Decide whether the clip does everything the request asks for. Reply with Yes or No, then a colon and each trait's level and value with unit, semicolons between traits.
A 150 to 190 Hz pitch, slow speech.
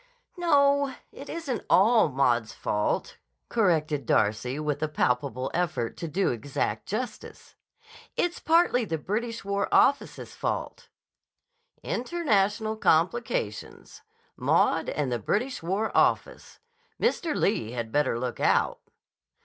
Yes: medium, 185 Hz; slow, 115 wpm